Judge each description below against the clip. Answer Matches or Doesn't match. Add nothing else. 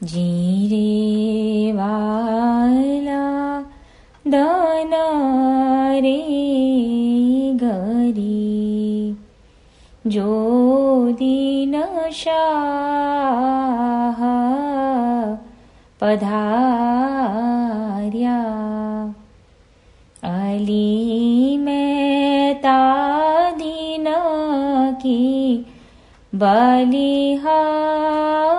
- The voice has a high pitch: Matches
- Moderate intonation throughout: Matches